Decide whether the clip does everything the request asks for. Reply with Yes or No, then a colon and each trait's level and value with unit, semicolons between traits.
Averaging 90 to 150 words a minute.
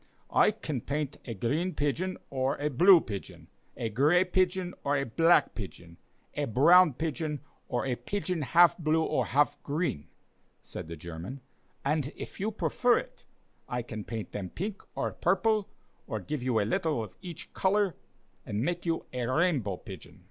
No: average, 170 wpm